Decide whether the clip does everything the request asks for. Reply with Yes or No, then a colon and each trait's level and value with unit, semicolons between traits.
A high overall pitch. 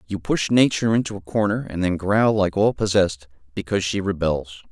No: low, 100 Hz